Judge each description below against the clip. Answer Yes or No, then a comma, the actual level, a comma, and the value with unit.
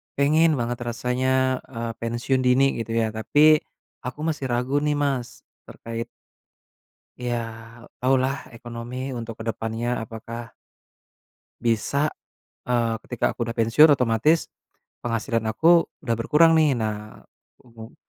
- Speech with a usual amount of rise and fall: Yes, average, 3.0 semitones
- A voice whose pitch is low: Yes, low, 120 Hz